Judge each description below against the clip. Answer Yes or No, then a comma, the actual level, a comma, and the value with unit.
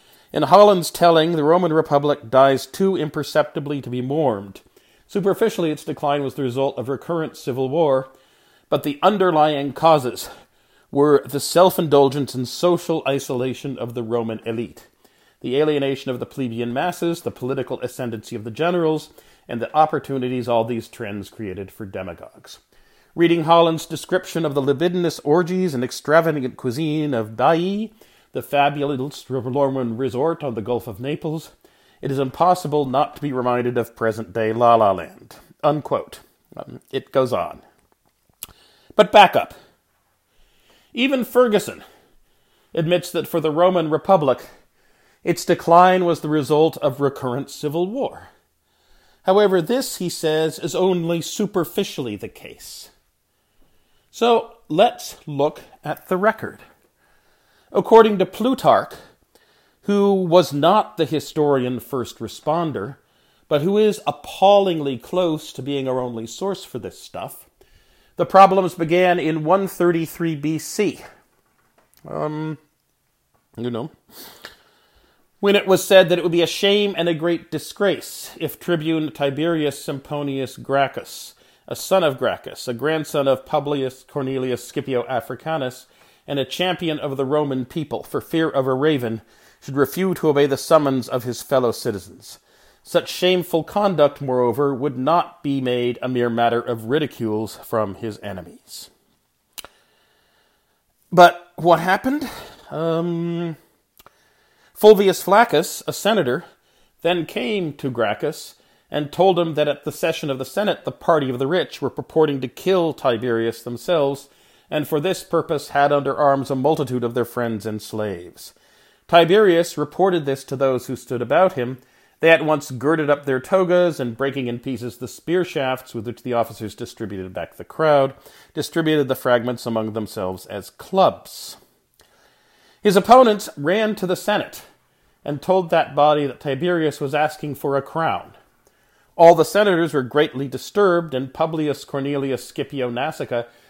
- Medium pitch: Yes, medium, 150 Hz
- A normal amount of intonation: Yes, average, 4.9 semitones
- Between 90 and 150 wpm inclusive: Yes, average, 145 wpm